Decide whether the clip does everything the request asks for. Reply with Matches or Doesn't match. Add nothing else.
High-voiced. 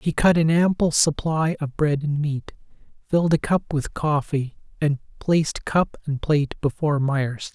Doesn't match